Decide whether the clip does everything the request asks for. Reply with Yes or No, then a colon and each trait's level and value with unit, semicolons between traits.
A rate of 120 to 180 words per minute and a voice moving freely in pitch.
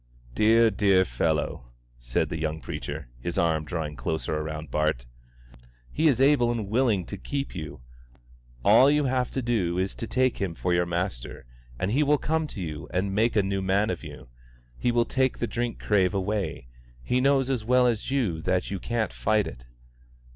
No: average, 190 wpm; wide, 6.3 semitones